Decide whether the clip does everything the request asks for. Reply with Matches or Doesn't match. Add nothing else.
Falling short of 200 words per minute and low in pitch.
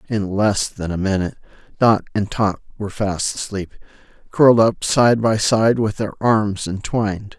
Matches